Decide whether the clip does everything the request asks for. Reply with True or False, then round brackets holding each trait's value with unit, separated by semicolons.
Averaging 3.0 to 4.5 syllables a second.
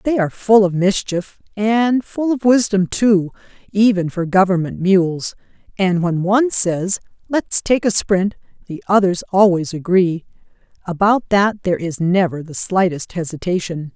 True (4.4 syllables/s)